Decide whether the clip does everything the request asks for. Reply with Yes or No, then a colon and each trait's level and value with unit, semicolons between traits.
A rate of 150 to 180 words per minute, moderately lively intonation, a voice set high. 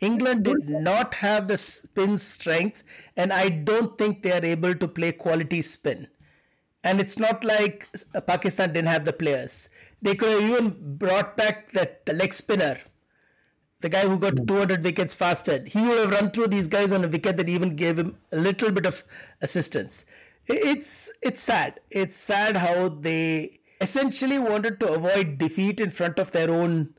Yes: average, 175 wpm; average, 3.5 semitones; high, 195 Hz